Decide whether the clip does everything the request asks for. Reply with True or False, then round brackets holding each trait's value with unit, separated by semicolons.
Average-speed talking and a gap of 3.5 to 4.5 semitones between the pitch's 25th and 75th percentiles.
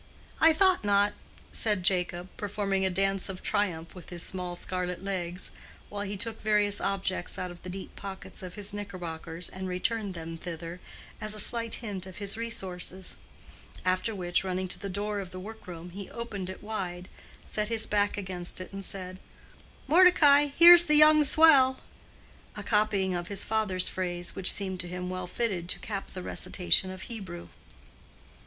False (170 wpm; 2.7 semitones)